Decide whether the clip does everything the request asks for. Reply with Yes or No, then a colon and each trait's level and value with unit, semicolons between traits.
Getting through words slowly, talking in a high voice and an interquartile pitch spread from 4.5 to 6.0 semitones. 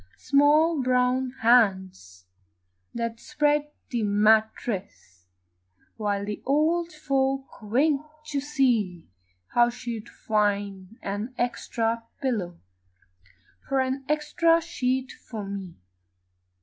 Yes: slow, 95 wpm; high, 240 Hz; average, 5.2 semitones